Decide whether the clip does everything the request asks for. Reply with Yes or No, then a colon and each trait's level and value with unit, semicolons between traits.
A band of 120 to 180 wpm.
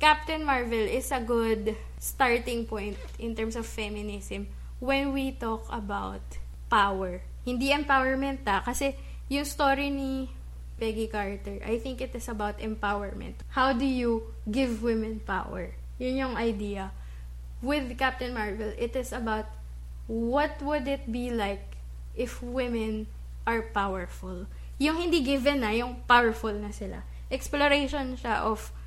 Yes: slow, 135 wpm